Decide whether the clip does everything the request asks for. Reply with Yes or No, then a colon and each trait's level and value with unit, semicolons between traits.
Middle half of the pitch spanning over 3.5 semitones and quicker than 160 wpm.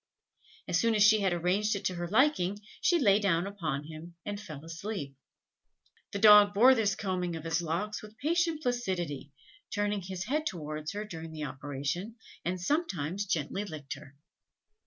Yes: average, 4.6 semitones; average, 170 wpm